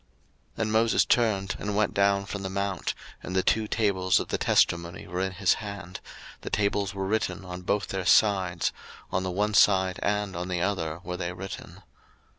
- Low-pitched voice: Yes, very low, 95 Hz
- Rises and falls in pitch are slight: Yes, narrow, 2.0 semitones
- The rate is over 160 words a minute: Yes, average, 195 wpm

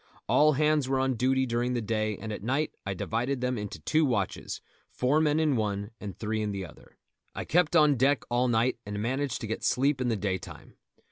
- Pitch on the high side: No, low, 125 Hz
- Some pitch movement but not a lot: Yes, average, 4.5 semitones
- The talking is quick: Yes, fast, 220 wpm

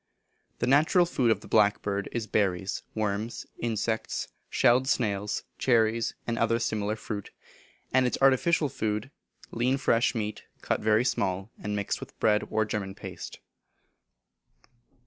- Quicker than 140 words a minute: No, slow, 135 wpm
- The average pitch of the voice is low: Yes, low, 110 Hz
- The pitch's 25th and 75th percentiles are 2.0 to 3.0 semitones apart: Yes, average, 2.7 semitones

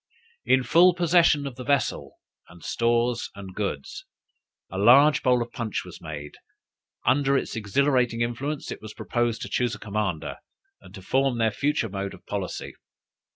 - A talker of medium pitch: No, low, 120 Hz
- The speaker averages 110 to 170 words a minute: Yes, average, 160 wpm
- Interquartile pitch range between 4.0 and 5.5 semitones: Yes, average, 5.2 semitones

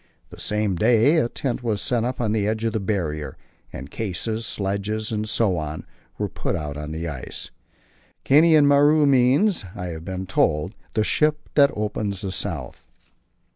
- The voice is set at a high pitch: No, low, 110 Hz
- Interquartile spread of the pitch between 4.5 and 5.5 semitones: Yes, average, 5.1 semitones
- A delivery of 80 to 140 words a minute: No, average, 175 wpm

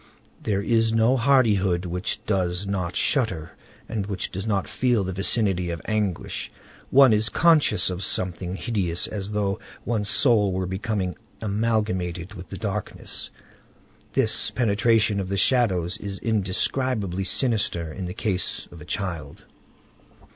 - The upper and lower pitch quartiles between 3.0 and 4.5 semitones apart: Yes, average, 3.4 semitones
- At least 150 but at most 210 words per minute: No, average, 140 wpm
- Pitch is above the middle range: No, low, 100 Hz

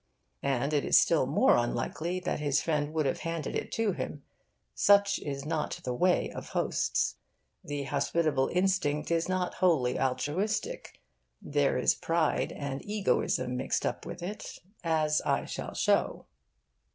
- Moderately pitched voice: Yes, medium, 155 Hz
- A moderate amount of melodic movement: Yes, average, 4.3 semitones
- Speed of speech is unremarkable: Yes, average, 150 wpm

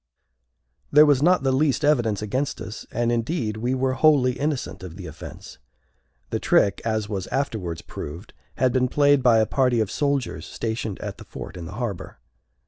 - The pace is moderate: Yes, average, 180 wpm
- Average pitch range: Yes, average, 4.4 semitones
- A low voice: Yes, low, 120 Hz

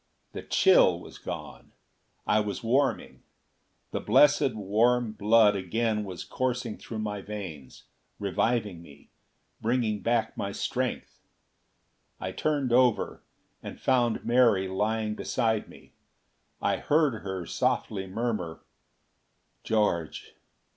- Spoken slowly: Yes, slow, 110 wpm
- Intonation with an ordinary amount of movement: Yes, average, 3.5 semitones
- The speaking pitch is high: No, low, 110 Hz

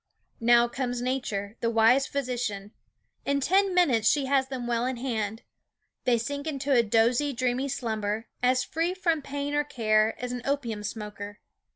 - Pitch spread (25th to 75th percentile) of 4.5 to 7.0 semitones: No, average, 3.8 semitones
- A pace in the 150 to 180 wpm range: Yes, average, 165 wpm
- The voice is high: Yes, high, 245 Hz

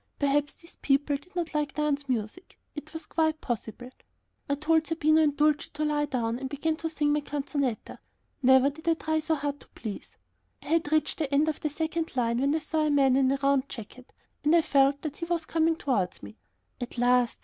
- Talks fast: Yes, fast, 220 wpm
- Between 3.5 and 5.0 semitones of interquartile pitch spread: No, average, 2.8 semitones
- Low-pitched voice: No, very high, 290 Hz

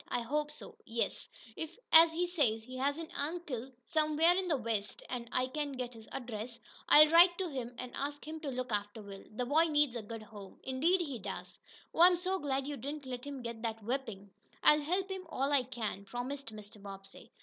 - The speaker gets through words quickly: Yes, fast, 215 wpm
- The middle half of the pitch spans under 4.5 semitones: No, average, 5.1 semitones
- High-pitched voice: Yes, very high, 265 Hz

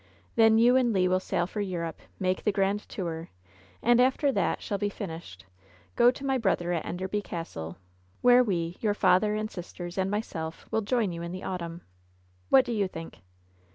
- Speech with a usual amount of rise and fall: Yes, average, 4.3 semitones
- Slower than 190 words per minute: No, average, 195 wpm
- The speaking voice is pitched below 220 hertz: Yes, high, 190 Hz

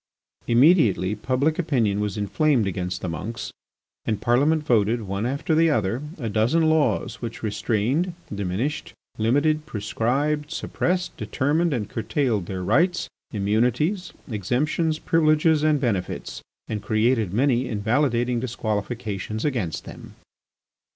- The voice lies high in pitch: No, low, 120 Hz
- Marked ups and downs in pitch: Yes, wide, 6.3 semitones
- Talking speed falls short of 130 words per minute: Yes, slow, 115 wpm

